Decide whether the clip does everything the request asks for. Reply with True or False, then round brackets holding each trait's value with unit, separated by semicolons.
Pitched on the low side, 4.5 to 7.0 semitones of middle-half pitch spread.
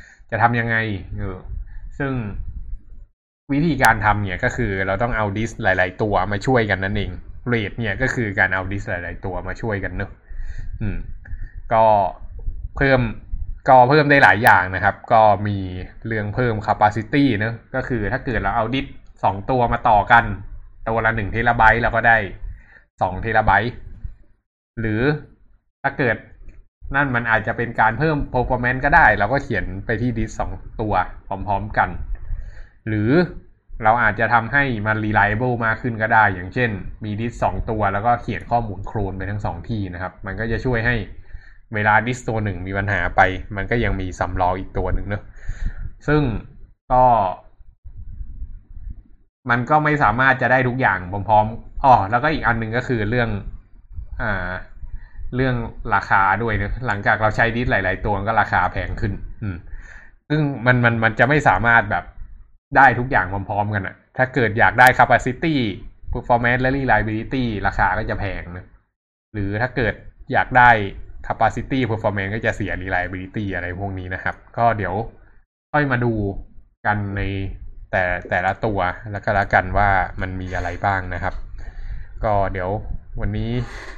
False (105 Hz; 3.8 semitones)